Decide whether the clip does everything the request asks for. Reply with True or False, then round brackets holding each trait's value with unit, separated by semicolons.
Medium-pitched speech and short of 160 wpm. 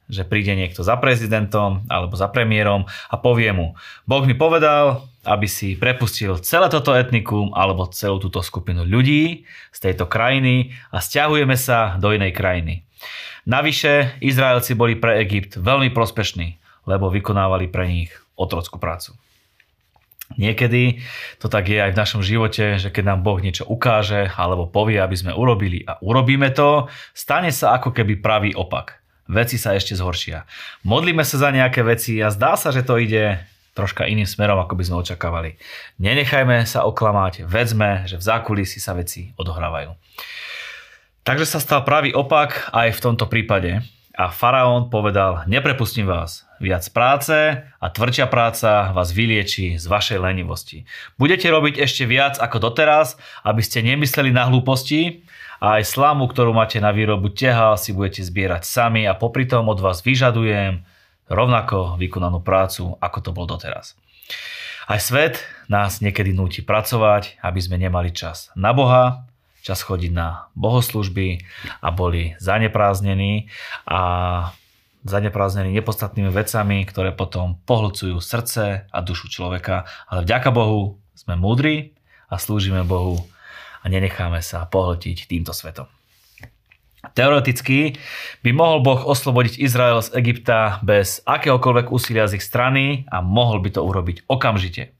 False (105 Hz; 145 wpm)